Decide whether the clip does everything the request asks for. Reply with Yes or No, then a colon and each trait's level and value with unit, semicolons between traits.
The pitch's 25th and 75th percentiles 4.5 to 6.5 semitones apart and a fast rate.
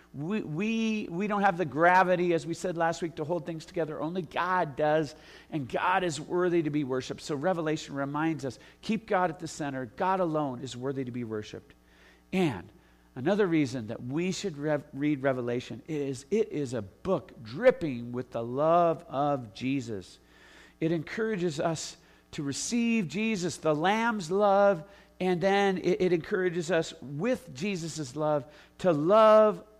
No: average, 4.9 semitones; average, 165 wpm